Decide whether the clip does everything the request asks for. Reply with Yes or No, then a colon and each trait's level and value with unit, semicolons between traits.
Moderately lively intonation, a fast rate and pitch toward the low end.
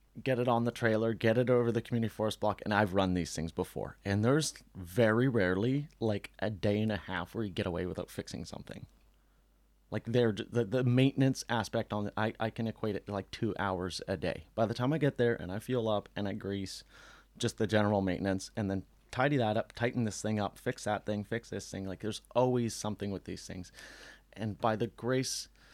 Yes: average, 3.2 semitones; fast, 225 wpm; low, 110 Hz